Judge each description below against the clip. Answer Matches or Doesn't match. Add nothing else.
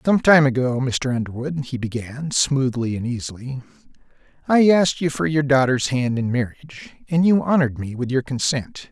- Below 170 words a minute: Doesn't match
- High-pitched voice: Doesn't match